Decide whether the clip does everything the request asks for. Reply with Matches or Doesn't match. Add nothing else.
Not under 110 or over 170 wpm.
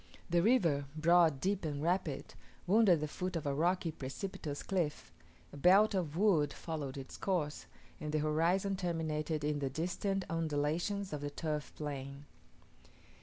Matches